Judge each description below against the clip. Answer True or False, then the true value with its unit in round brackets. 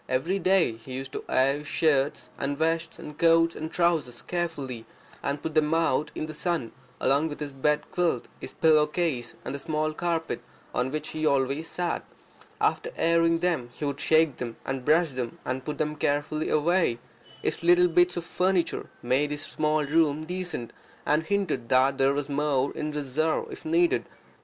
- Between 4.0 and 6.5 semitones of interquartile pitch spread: False (3.2 semitones)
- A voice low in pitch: False (150 Hz)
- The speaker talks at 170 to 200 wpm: True (180 wpm)